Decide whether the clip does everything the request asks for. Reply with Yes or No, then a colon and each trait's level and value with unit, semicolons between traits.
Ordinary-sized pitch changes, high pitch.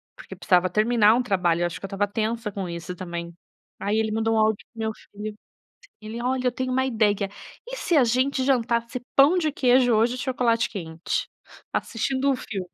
Yes: average, 4.1 semitones; high, 225 Hz